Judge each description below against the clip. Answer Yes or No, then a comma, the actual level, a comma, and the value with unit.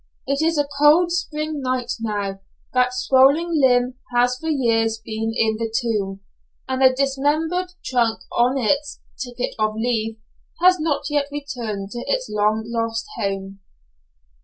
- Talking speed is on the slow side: No, average, 145 wpm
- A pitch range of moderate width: Yes, average, 4.5 semitones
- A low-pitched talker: No, very high, 250 Hz